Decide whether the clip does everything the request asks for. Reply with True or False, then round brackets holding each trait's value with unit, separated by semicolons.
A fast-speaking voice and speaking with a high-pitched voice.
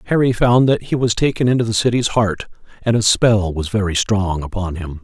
False (215 wpm; 105 Hz)